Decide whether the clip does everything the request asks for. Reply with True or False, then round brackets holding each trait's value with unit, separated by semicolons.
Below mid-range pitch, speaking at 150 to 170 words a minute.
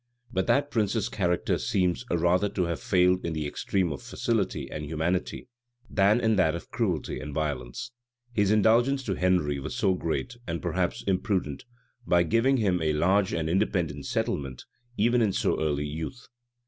True (90 Hz; 160 wpm)